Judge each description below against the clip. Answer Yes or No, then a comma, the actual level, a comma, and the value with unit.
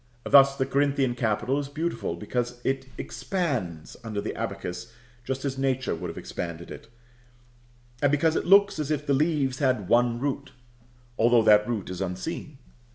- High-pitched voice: No, low, 130 Hz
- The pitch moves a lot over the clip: No, average, 4.1 semitones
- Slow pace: No, average, 160 wpm